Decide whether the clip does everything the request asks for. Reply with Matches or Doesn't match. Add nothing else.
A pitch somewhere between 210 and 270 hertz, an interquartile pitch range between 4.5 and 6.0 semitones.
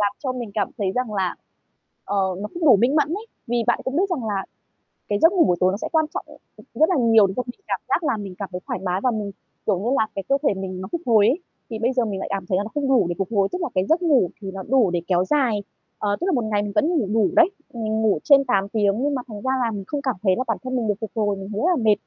Matches